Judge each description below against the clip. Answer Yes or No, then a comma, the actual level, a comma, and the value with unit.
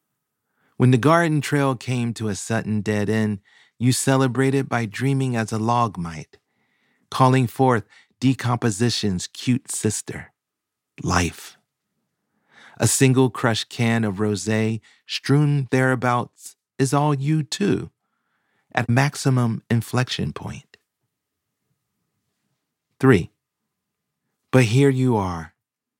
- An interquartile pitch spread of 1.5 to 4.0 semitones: Yes, average, 3.3 semitones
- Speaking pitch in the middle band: No, low, 120 Hz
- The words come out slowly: Yes, slow, 105 wpm